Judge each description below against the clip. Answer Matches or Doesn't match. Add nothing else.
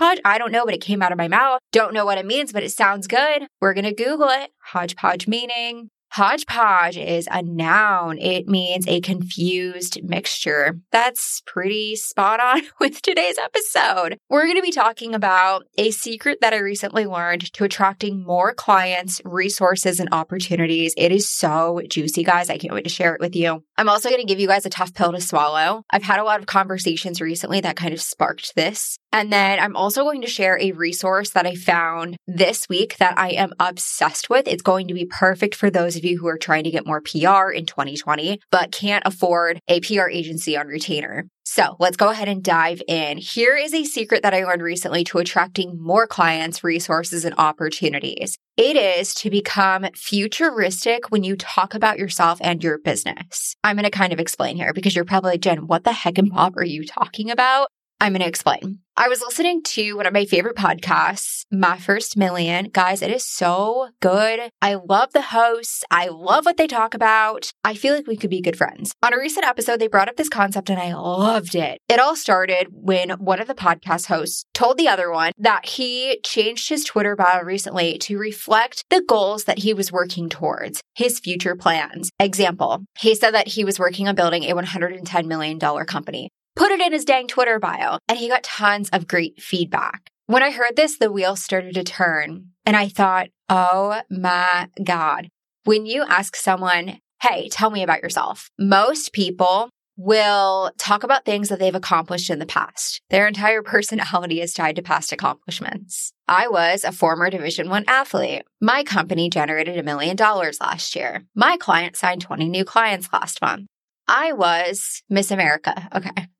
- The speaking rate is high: Doesn't match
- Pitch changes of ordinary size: Matches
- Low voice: Doesn't match